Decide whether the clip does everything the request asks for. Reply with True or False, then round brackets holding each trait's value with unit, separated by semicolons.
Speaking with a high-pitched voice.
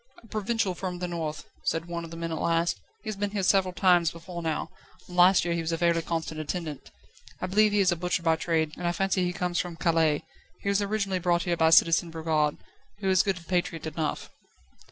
False (175 Hz)